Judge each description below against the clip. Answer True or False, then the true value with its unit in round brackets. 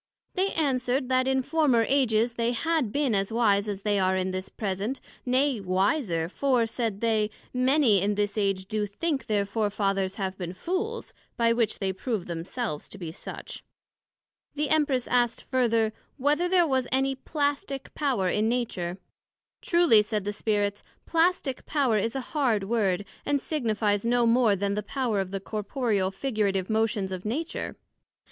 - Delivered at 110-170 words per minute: True (165 wpm)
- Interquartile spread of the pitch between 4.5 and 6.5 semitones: True (5.0 semitones)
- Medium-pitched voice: False (225 Hz)